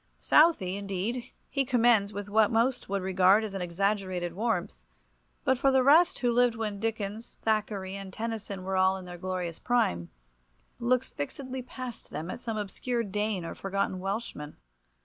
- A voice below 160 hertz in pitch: No, high, 205 Hz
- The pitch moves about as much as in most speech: Yes, average, 4.0 semitones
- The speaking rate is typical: Yes, average, 165 wpm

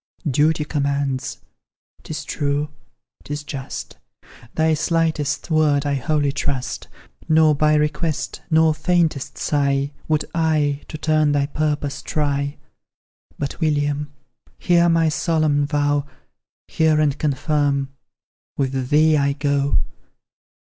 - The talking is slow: Yes, slow, 110 wpm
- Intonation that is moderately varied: No, narrow, 1.6 semitones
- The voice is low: No, medium, 150 Hz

